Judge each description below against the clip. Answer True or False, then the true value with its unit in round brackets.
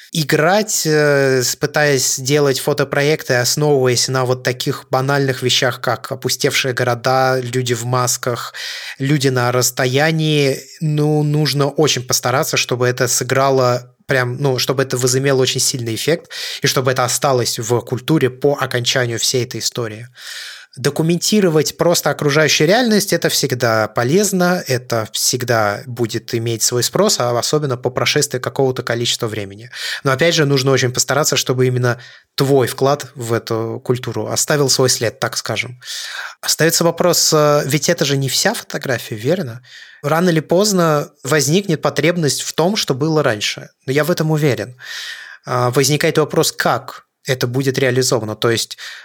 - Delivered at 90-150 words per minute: True (140 wpm)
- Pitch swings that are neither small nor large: True (3.4 semitones)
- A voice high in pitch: False (135 Hz)